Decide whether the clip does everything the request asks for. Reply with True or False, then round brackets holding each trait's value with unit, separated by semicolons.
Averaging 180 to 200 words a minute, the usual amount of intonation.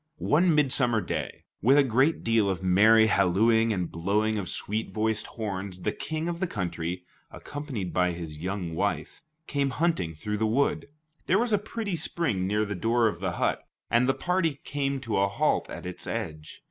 False (185 wpm; 7.0 semitones)